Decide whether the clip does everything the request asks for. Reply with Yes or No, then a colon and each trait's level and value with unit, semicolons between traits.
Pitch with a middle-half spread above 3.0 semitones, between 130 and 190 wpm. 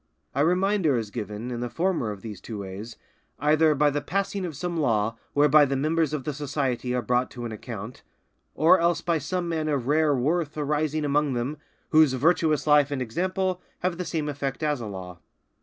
No: average, 4.6 semitones; average, 200 wpm